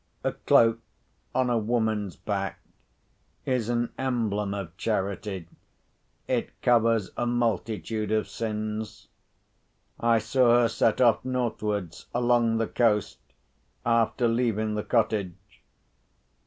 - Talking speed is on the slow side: Yes, slow, 105 wpm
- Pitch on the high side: No, low, 115 Hz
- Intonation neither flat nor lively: No, narrow, 2.1 semitones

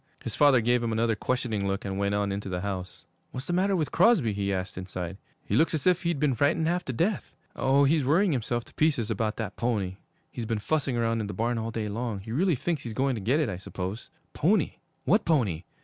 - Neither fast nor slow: No, fast, 240 wpm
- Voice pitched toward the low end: Yes, low, 120 Hz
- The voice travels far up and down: Yes, wide, 6.5 semitones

